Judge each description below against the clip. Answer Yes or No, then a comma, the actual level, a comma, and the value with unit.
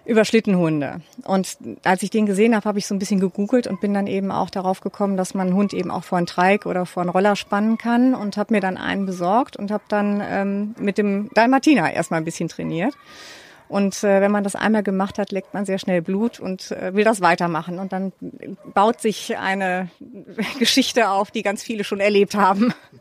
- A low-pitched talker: No, high, 200 Hz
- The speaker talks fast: Yes, fast, 210 wpm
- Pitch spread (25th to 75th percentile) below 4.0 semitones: Yes, narrow, 2.5 semitones